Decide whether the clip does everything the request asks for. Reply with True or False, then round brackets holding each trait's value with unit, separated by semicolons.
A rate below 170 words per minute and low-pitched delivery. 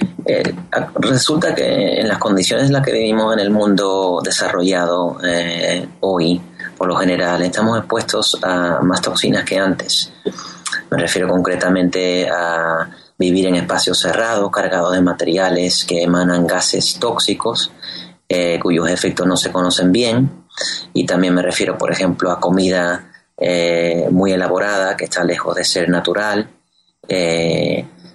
True (140 wpm; 90 Hz)